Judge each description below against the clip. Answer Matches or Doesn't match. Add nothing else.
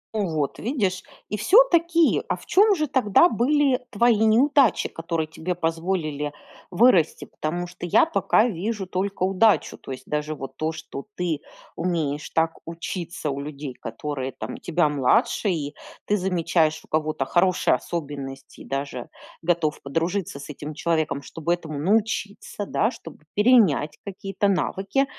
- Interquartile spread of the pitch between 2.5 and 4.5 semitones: Doesn't match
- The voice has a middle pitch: Matches